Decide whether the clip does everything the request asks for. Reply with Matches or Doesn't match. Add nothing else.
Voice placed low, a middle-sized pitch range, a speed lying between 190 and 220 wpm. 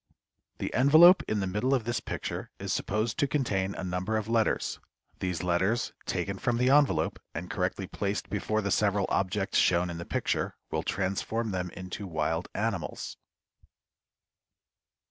Doesn't match